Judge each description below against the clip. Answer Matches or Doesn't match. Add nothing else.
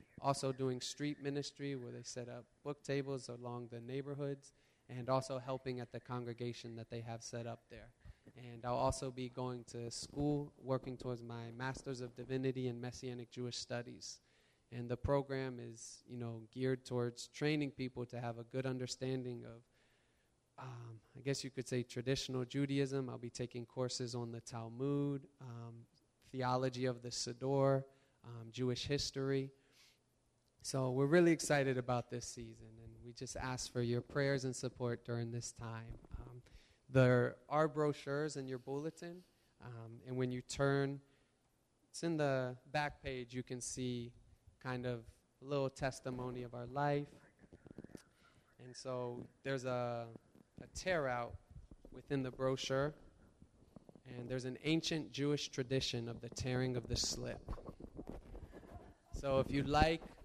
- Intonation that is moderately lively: Doesn't match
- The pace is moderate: Matches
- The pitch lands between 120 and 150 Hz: Matches